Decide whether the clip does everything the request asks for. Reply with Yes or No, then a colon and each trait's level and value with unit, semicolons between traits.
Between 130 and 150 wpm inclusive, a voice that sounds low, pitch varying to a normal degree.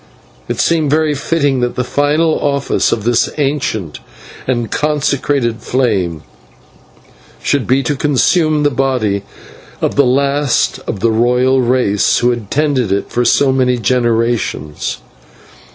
Yes: slow, 135 wpm; low, 130 Hz; average, 3.4 semitones